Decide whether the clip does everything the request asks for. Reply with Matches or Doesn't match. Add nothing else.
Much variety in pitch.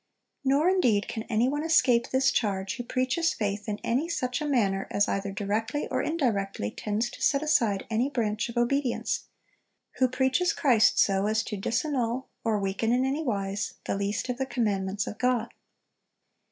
Doesn't match